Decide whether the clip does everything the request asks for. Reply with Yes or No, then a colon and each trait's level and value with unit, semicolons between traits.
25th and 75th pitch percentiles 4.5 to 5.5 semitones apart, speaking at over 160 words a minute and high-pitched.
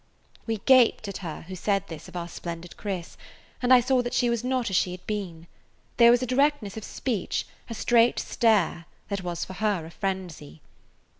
Yes: average, 5.2 semitones; average, 200 wpm; high, 200 Hz